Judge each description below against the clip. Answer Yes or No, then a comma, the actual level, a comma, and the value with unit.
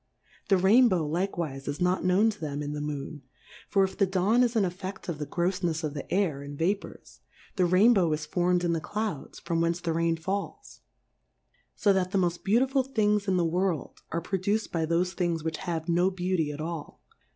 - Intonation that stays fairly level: No, average, 3.2 semitones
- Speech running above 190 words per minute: Yes, fast, 205 wpm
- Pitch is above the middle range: No, medium, 180 Hz